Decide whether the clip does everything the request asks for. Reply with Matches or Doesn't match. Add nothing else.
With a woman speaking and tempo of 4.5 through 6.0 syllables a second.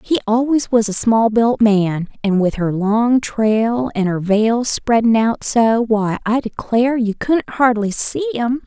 Doesn't match